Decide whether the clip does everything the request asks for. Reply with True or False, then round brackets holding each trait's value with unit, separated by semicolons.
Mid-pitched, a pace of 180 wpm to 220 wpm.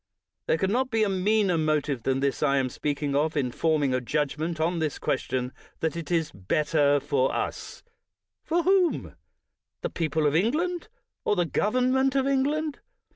True (160 Hz; 185 wpm)